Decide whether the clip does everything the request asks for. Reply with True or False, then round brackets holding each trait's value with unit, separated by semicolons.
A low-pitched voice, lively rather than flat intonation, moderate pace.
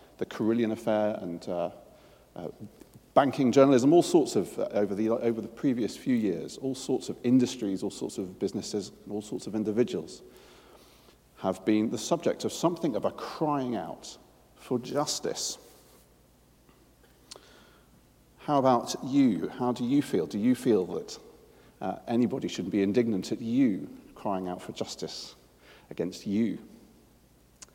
True (120 Hz; 6.1 semitones; 150 wpm)